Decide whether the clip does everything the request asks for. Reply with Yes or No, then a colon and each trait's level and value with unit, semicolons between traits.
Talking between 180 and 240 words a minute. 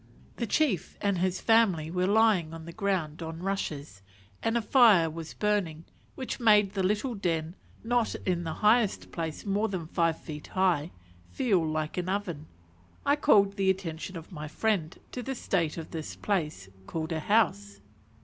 No: average, 170 wpm